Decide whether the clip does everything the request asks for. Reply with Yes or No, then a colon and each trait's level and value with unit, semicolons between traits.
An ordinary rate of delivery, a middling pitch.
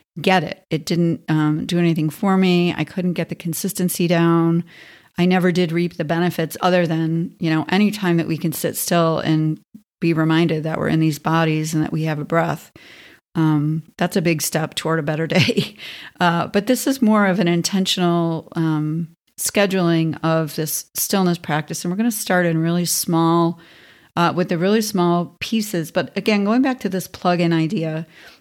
Yes: average, 190 wpm; medium, 170 Hz